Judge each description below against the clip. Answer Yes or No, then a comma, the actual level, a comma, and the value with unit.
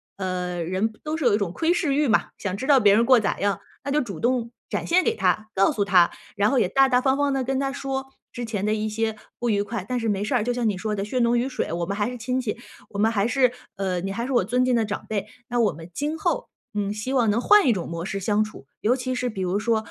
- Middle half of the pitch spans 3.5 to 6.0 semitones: Yes, average, 4.2 semitones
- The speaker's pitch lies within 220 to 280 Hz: Yes, high, 225 Hz